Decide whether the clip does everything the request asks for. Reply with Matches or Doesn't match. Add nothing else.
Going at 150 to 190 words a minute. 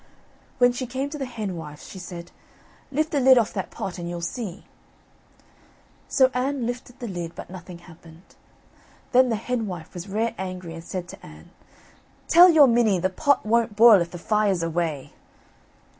Matches